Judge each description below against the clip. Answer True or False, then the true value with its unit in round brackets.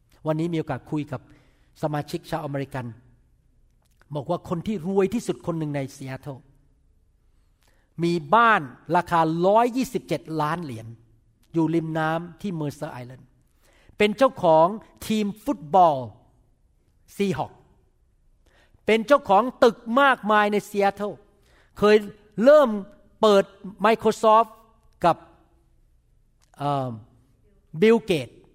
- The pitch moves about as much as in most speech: False (7.7 semitones)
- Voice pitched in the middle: True (165 Hz)